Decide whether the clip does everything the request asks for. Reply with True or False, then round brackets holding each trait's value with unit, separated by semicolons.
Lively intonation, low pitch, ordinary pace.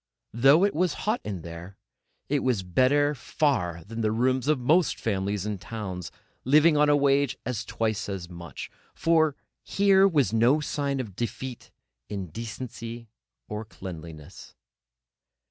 True (6.8 semitones; 120 Hz; 145 wpm)